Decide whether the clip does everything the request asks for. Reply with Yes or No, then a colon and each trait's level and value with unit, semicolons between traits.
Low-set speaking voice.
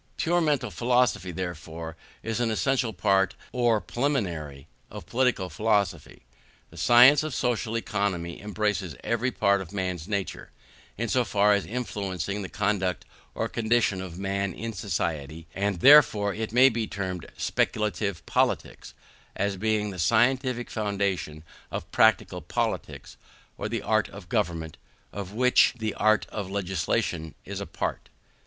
Yes: low, 100 Hz